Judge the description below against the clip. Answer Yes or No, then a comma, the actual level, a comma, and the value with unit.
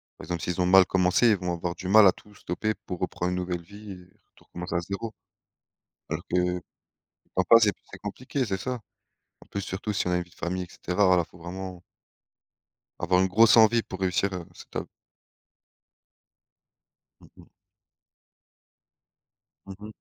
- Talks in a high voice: No, very low, 95 Hz